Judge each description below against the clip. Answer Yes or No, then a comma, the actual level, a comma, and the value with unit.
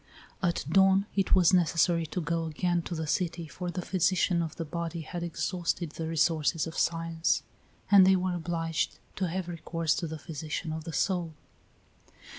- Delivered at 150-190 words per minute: Yes, average, 175 wpm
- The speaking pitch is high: No, medium, 170 Hz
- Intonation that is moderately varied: No, narrow, 1.8 semitones